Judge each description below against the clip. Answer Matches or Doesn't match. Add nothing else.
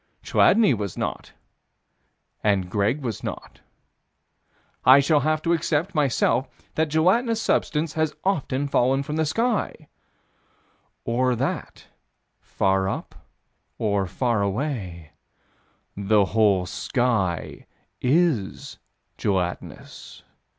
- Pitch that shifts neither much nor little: Doesn't match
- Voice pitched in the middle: Doesn't match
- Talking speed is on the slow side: Matches